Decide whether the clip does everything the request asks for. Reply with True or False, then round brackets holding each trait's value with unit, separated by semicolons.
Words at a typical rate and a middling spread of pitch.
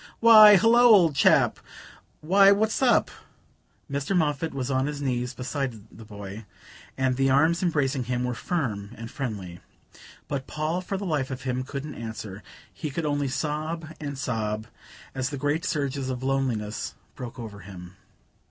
True (160 wpm; 4.4 semitones)